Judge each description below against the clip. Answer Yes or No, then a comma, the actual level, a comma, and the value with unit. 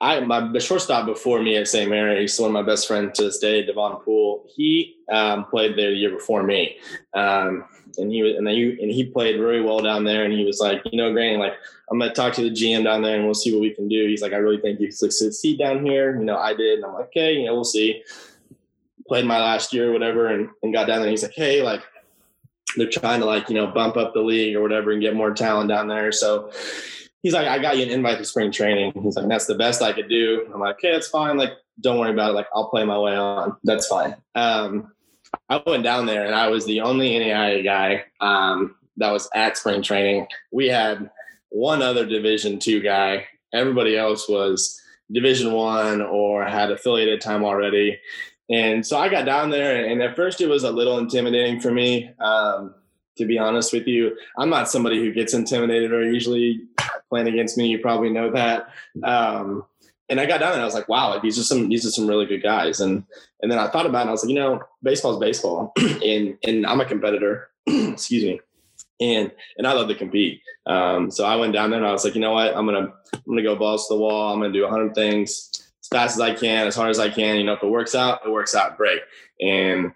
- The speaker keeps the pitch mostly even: Yes, narrow, 2.3 semitones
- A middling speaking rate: No, fast, 245 wpm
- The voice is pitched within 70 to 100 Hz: No, low, 110 Hz